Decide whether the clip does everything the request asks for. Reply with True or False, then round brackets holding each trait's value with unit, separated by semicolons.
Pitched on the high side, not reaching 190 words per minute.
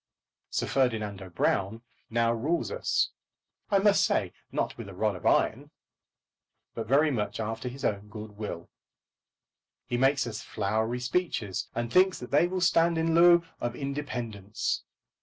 False (120 Hz; 150 wpm)